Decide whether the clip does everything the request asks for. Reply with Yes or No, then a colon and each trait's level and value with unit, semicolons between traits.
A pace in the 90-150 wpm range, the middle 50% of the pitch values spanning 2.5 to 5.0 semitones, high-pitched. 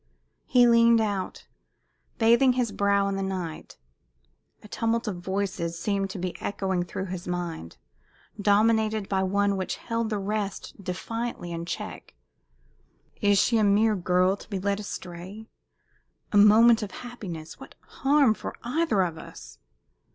Yes: average, 145 wpm; average, 3.2 semitones; high, 200 Hz